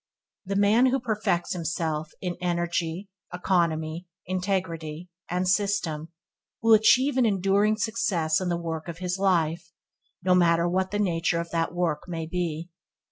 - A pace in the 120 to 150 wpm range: Yes, average, 145 wpm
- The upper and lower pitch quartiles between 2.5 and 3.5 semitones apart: Yes, average, 2.9 semitones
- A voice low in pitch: No, medium, 180 Hz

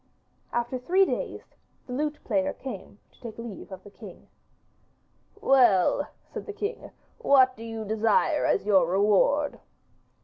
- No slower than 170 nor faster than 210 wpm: No, average, 140 wpm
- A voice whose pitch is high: Yes, high, 240 Hz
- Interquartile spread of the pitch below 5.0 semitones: No, wide, 5.4 semitones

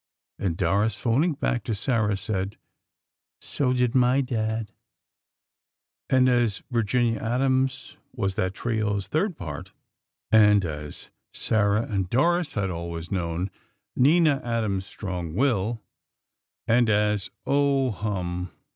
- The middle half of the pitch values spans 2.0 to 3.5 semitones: No, average, 4.6 semitones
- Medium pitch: No, low, 110 Hz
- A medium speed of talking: No, slow, 115 wpm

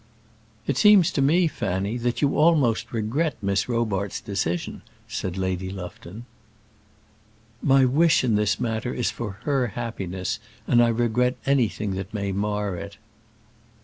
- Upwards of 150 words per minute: No, average, 140 wpm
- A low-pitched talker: Yes, low, 115 Hz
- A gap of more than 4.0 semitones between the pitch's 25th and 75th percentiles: Yes, average, 4.9 semitones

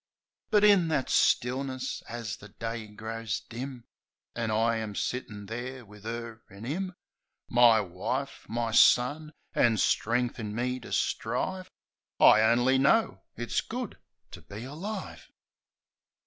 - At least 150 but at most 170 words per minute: No, average, 140 wpm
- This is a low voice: Yes, low, 120 Hz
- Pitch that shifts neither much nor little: Yes, average, 3.1 semitones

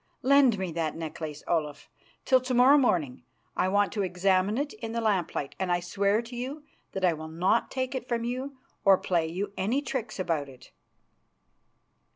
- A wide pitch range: Yes, wide, 6.2 semitones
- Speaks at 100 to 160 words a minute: No, average, 185 wpm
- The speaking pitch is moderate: No, high, 200 Hz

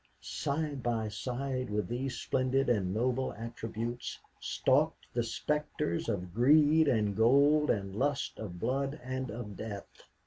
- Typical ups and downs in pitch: Yes, average, 4.0 semitones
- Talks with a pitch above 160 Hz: No, low, 125 Hz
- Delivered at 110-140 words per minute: Yes, slow, 135 wpm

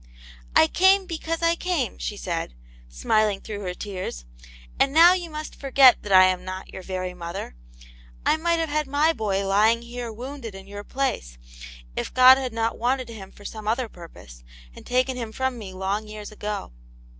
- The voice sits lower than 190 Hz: No, high, 225 Hz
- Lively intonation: Yes, wide, 5.9 semitones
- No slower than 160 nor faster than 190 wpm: Yes, average, 185 wpm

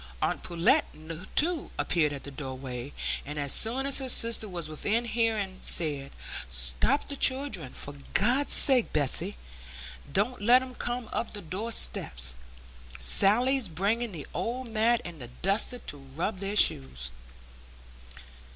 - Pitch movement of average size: No, wide, 8.9 semitones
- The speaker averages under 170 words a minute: Yes, average, 140 wpm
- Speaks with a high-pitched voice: Yes, high, 200 Hz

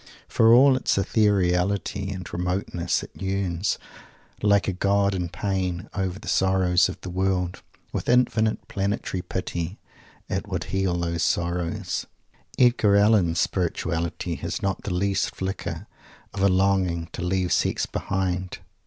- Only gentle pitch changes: Yes, narrow, 2.0 semitones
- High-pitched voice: No, very low, 95 Hz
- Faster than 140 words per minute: No, slow, 135 wpm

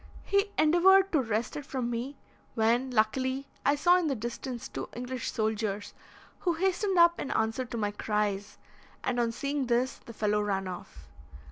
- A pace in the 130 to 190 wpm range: Yes, average, 170 wpm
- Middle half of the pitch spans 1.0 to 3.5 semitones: No, average, 5.0 semitones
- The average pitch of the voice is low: No, high, 245 Hz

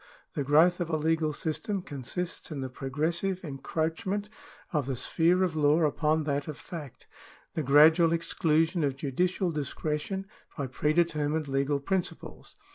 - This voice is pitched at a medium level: Yes, medium, 155 Hz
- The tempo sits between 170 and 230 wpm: No, average, 145 wpm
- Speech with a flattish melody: No, average, 3.0 semitones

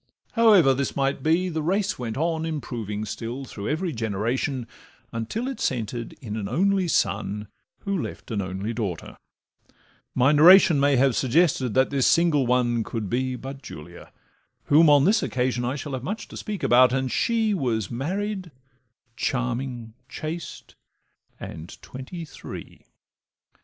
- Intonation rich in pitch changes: Yes, wide, 5.8 semitones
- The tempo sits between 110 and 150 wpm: Yes, average, 145 wpm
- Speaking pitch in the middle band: No, low, 130 Hz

